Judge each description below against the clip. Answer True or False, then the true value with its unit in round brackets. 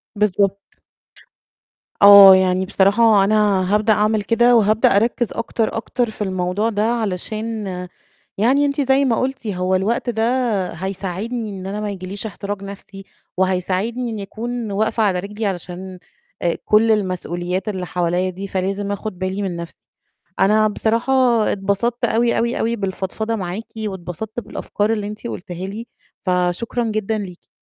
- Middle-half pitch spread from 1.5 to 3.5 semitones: True (3.0 semitones)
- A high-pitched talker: True (205 Hz)